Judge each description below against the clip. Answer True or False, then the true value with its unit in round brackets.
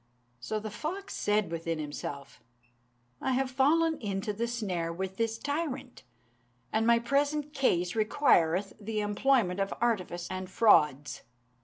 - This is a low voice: False (215 Hz)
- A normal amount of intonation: False (6.5 semitones)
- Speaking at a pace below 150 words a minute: True (135 wpm)